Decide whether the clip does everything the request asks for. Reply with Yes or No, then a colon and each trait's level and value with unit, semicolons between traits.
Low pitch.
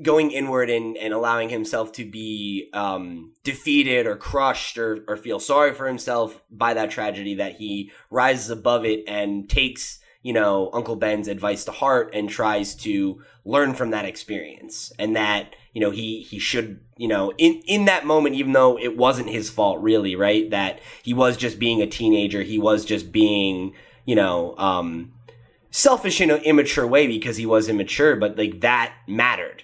Yes: low, 115 Hz